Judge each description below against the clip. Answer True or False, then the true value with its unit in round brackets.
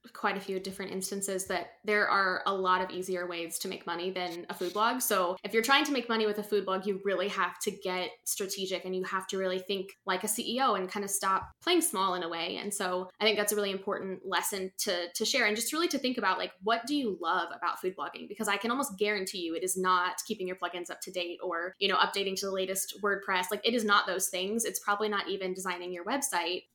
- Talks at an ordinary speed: False (260 wpm)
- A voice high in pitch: True (195 Hz)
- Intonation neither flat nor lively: False (2.2 semitones)